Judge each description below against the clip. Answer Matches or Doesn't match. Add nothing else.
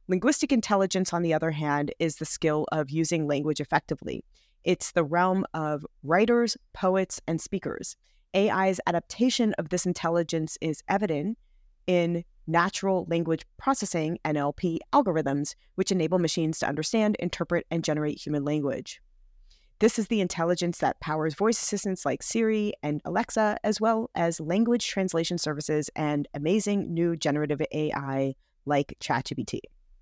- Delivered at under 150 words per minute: Matches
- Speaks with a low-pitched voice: Doesn't match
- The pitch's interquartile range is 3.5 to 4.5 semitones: Matches